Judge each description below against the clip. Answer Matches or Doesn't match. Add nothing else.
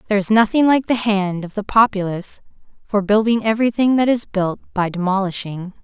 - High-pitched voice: Matches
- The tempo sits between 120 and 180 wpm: Matches